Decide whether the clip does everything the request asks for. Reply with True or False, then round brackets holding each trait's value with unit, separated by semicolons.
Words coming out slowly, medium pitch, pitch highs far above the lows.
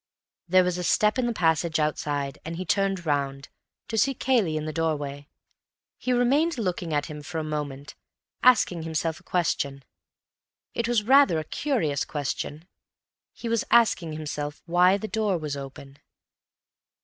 False (160 wpm; 165 Hz; 6.2 semitones)